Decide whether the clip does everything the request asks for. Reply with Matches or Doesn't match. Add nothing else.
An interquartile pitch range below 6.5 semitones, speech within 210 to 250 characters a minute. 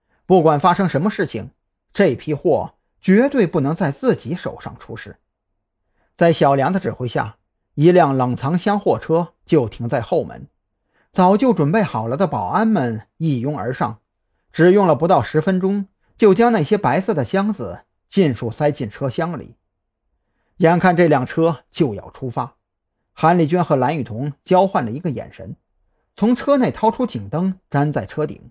Doesn't match